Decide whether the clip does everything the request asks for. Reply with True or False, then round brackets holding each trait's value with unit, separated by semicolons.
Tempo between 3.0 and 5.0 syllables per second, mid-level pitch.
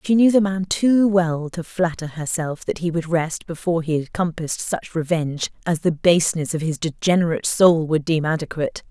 False (5.3 syllables/s; 170 Hz)